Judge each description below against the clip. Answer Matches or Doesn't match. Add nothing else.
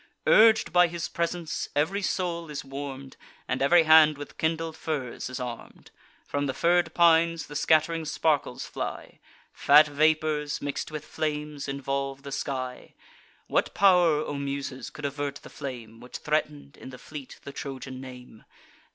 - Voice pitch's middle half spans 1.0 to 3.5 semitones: Matches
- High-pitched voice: Doesn't match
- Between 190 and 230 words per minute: Doesn't match